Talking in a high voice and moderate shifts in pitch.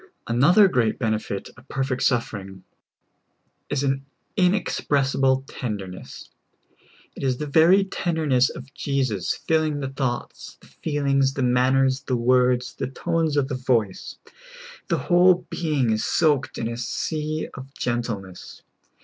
No: low, 135 Hz; average, 3.6 semitones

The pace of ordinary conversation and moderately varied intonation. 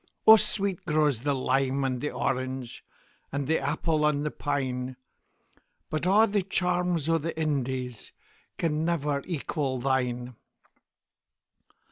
No: slow, 110 wpm; average, 3.9 semitones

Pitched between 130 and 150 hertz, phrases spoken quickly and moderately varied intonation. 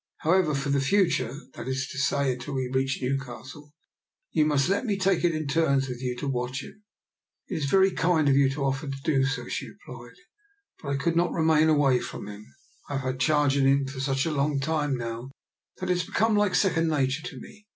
Yes: medium, 140 Hz; fast, 235 wpm; average, 3.3 semitones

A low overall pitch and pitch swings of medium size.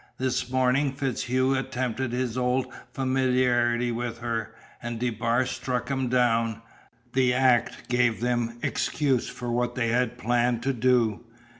No: low, 125 Hz; narrow, 1.5 semitones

